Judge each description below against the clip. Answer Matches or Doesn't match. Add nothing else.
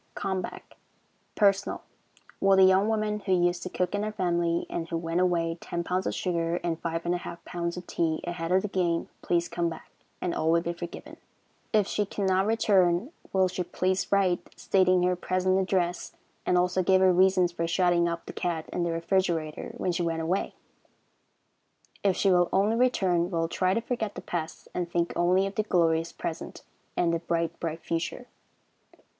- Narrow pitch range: Matches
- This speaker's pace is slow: Doesn't match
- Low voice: Doesn't match